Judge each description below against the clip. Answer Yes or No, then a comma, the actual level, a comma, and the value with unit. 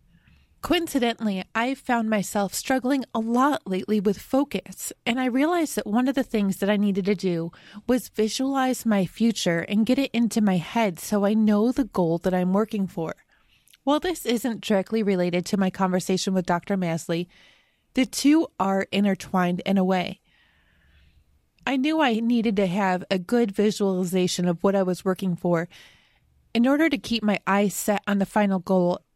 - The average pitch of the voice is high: Yes, high, 205 Hz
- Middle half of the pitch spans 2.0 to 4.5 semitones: Yes, average, 4.1 semitones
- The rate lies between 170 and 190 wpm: Yes, average, 175 wpm